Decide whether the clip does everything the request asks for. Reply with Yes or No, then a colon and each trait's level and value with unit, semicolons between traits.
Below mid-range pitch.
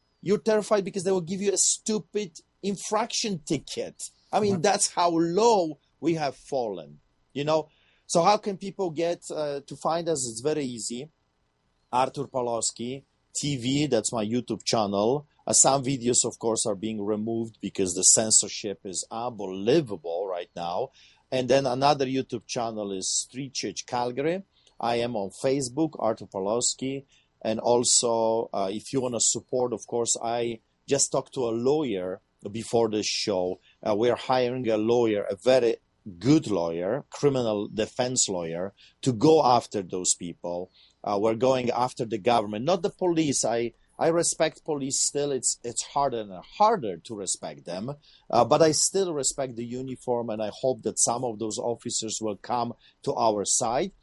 Yes: low, 125 Hz